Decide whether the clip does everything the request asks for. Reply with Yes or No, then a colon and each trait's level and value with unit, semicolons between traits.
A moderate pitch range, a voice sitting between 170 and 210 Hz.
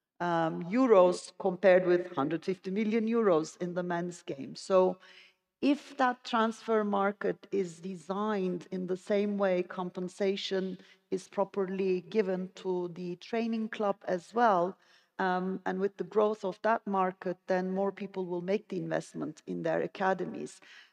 No: narrow, 1.9 semitones; high, 190 Hz